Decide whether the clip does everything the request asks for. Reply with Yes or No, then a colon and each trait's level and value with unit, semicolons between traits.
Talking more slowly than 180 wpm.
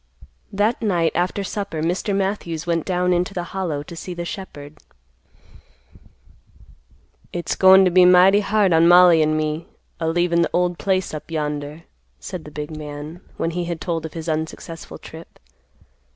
Yes: average, 165 wpm